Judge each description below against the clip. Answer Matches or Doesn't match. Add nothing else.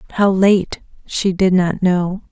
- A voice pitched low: Doesn't match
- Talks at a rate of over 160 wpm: Doesn't match